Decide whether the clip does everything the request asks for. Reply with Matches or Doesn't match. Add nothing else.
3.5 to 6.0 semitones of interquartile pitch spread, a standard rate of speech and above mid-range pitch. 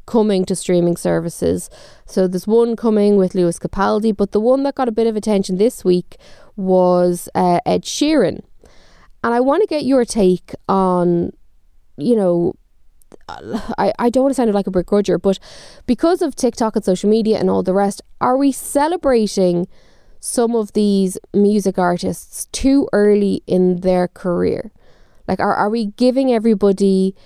Matches